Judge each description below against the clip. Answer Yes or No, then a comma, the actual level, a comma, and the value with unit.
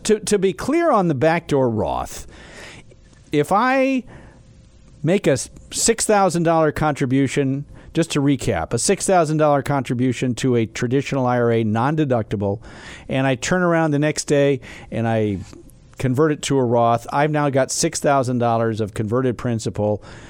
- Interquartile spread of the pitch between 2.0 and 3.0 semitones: No, average, 5.2 semitones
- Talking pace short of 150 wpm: Yes, average, 140 wpm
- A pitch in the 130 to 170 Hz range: Yes, low, 135 Hz